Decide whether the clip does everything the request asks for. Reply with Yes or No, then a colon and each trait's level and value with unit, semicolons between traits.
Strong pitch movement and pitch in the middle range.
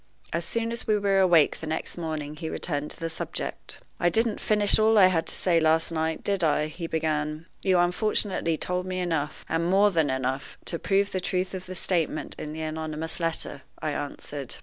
No: average, 3.0 semitones; medium, 165 Hz